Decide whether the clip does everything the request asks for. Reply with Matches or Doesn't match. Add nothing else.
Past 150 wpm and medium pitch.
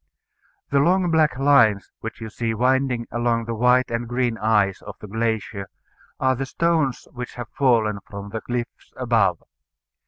Doesn't match